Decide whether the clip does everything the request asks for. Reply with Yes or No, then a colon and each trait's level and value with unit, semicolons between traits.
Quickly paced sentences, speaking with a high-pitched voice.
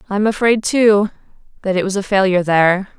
No: average, 180 wpm; high, 200 Hz